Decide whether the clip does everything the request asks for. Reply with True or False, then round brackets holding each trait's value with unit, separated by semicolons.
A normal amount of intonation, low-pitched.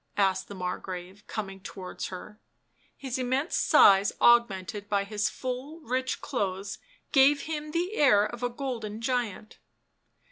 False (4.7 semitones; 220 Hz)